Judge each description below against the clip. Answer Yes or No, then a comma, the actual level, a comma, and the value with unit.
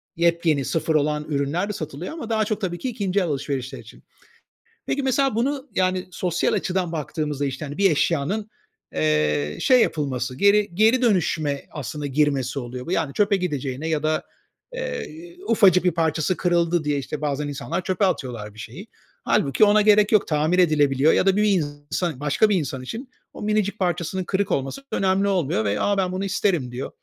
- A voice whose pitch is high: No, medium, 170 Hz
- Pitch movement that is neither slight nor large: No, wide, 5.8 semitones